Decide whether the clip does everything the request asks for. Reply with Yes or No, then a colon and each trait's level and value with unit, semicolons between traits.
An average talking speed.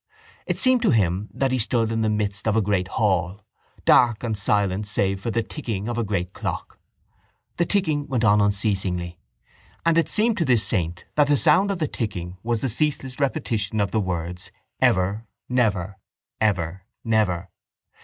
Yes: average, 175 wpm